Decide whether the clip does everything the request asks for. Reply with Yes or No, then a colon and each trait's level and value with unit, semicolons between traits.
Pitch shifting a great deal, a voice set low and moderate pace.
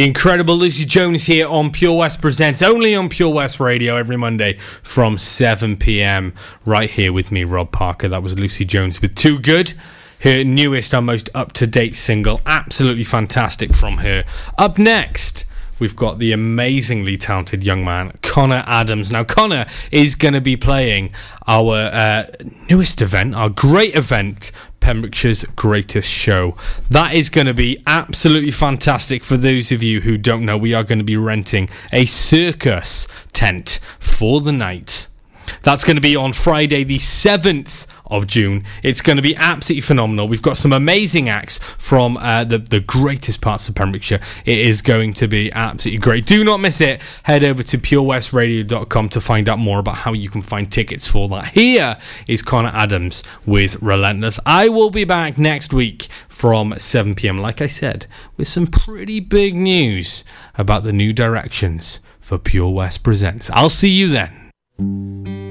Yes: wide, 5.7 semitones; low, 115 Hz; average, 170 wpm